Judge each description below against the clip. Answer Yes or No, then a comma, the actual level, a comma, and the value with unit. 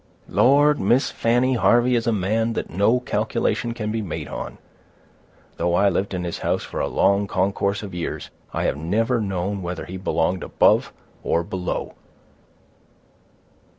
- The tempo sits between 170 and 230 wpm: No, average, 155 wpm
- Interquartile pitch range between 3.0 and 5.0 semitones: Yes, average, 4.1 semitones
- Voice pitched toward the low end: Yes, low, 100 Hz